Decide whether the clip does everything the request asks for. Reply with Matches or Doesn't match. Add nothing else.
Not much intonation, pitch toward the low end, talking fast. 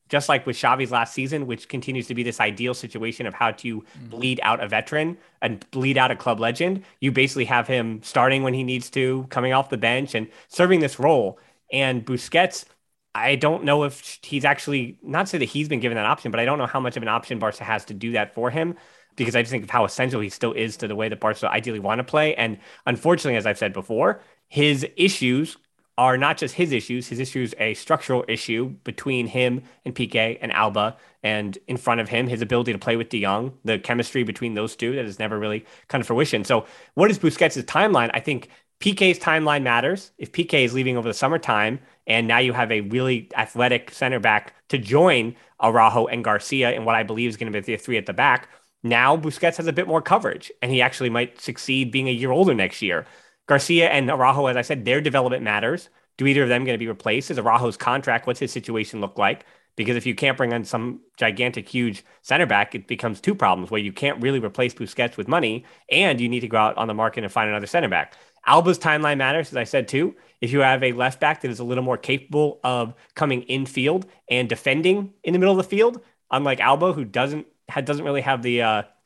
Doesn't match